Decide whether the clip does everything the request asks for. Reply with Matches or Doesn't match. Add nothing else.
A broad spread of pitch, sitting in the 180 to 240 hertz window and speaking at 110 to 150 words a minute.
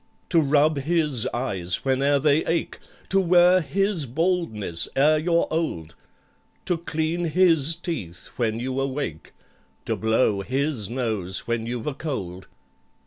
Doesn't match